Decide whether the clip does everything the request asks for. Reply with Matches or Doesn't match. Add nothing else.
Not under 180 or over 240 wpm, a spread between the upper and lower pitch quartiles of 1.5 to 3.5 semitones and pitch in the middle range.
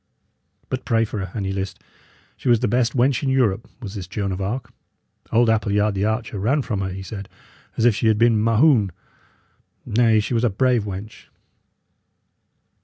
Doesn't match